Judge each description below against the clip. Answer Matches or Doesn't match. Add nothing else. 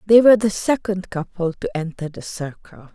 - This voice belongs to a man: Doesn't match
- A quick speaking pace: Doesn't match